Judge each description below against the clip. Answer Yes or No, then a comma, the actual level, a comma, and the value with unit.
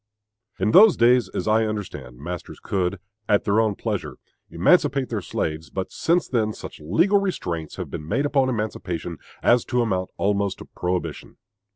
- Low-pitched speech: Yes, low, 105 Hz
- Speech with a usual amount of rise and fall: No, wide, 5.7 semitones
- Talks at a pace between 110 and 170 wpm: Yes, average, 165 wpm